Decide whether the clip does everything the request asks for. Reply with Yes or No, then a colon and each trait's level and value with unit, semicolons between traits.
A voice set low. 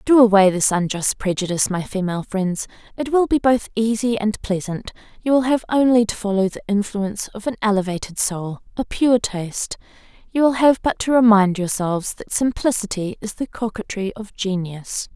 No: high, 215 Hz